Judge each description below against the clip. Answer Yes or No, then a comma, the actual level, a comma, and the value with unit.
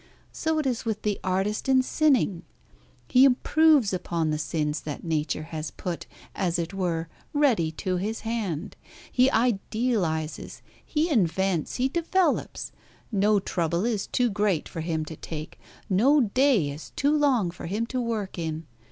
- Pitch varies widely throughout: Yes, wide, 7.1 semitones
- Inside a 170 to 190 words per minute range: No, average, 155 wpm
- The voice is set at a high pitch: Yes, high, 200 Hz